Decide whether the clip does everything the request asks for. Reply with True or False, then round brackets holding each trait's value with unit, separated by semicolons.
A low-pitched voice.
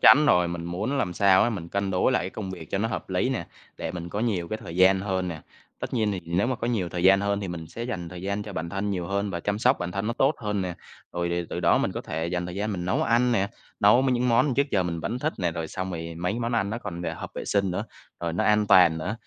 True (95 Hz)